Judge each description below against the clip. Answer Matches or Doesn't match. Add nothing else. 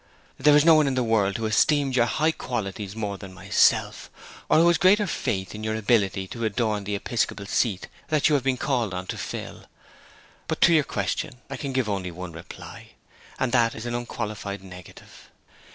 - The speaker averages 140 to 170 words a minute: Doesn't match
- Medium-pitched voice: Doesn't match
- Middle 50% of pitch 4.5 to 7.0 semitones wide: Matches